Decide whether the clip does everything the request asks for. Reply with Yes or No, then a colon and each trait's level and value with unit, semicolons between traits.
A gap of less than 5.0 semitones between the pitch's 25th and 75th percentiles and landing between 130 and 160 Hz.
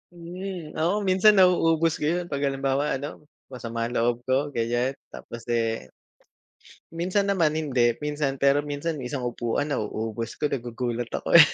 No: wide, 5.4 semitones; medium, 140 Hz